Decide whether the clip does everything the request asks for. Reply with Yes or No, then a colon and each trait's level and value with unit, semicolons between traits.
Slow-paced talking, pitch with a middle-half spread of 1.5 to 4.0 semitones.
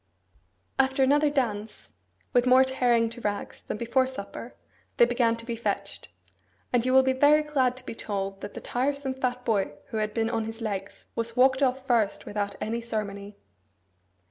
No: average, 180 wpm; average, 3.4 semitones